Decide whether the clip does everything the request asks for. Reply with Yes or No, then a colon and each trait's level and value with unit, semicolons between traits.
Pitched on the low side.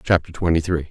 Yes: very low, 80 Hz